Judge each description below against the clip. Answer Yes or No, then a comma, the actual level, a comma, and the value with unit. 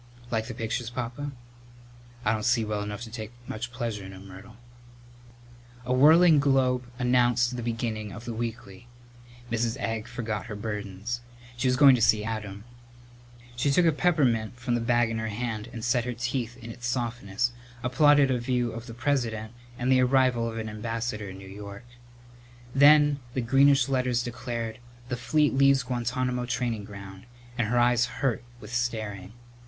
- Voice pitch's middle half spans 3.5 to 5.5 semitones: No, narrow, 2.5 semitones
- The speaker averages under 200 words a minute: Yes, average, 170 wpm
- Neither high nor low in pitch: No, low, 120 Hz